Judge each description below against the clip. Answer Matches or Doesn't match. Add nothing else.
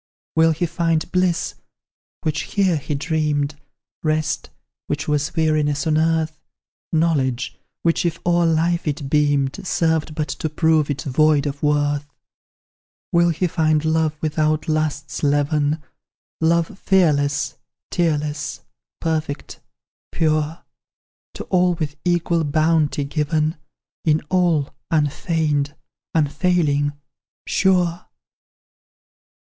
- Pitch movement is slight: Matches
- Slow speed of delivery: Matches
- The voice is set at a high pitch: Doesn't match